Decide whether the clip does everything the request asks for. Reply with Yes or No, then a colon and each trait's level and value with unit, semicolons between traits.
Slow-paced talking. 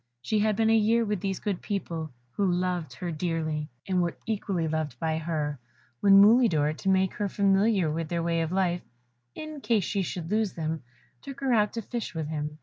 No: fast, 205 wpm